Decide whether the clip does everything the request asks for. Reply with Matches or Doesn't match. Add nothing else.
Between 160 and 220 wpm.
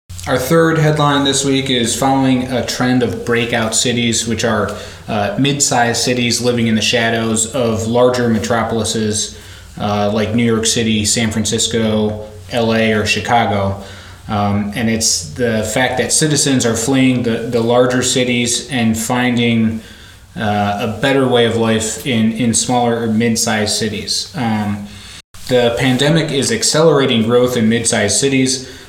Doesn't match